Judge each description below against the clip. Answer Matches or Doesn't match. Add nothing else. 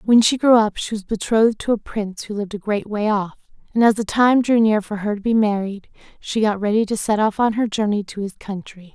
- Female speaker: Matches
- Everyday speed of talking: Doesn't match